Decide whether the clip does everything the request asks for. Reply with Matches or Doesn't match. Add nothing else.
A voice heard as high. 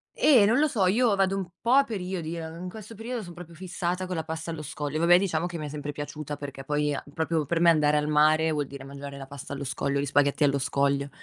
Doesn't match